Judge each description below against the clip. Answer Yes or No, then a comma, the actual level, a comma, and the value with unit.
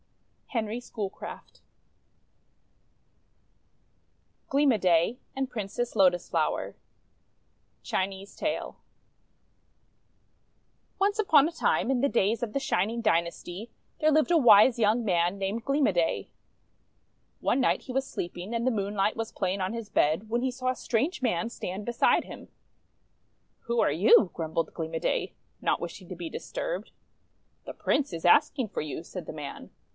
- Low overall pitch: No, high, 220 Hz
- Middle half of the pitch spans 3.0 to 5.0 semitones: No, wide, 5.6 semitones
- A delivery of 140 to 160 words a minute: Yes, average, 150 wpm